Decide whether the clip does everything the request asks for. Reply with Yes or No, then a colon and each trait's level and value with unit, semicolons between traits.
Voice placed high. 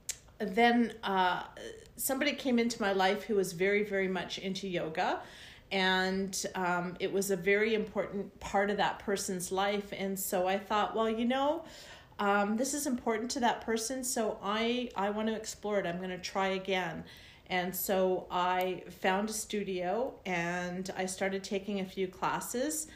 Yes: high, 195 Hz